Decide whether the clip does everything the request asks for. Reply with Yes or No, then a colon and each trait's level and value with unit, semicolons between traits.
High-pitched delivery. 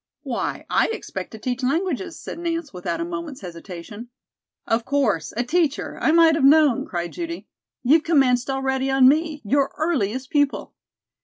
Yes: very high, 275 Hz